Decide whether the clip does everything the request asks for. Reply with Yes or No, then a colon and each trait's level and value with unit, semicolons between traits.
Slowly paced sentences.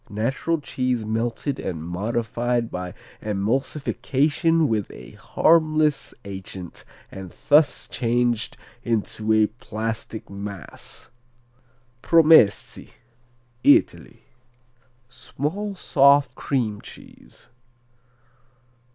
Yes: slow, 75 wpm